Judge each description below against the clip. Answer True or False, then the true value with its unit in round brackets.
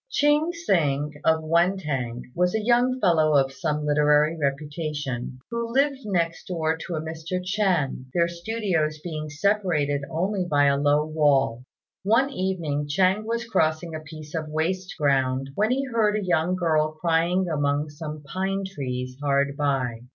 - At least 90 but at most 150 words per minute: False (160 wpm)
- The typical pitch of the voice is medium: True (160 Hz)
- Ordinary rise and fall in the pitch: True (4.5 semitones)